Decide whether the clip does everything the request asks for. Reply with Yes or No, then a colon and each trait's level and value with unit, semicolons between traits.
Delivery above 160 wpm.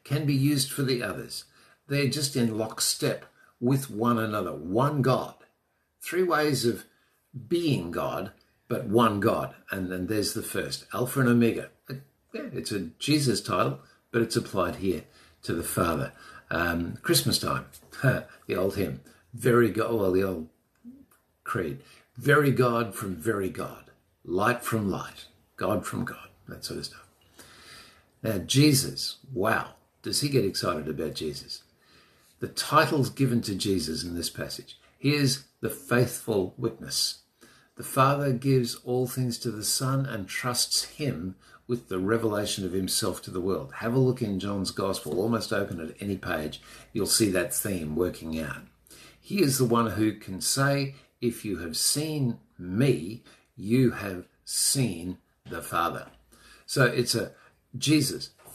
No: average, 155 wpm